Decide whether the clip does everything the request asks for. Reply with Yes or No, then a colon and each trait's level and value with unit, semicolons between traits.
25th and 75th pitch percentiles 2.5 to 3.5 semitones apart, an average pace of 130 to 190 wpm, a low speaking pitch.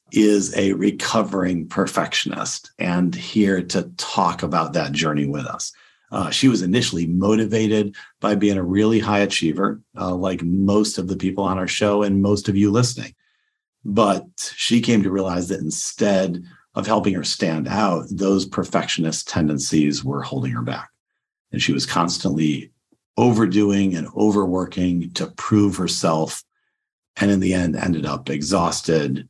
Yes: average, 2.8 semitones; average, 150 wpm; very low, 95 Hz